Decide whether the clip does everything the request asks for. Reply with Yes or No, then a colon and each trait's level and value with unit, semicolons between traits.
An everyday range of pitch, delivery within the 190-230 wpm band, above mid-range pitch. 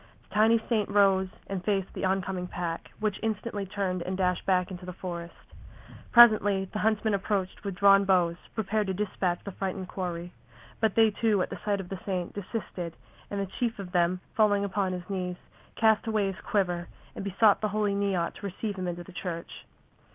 No: narrow, 2.3 semitones; average, 195 wpm; high, 195 Hz